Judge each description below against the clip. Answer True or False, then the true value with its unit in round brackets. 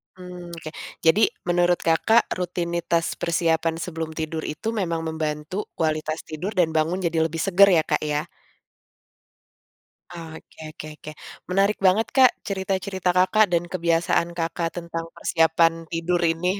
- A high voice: False (170 Hz)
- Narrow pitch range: True (2.1 semitones)